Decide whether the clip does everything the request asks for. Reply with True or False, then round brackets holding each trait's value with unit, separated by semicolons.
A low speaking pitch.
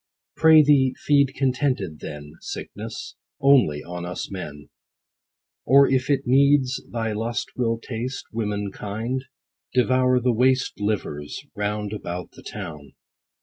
True (115 Hz)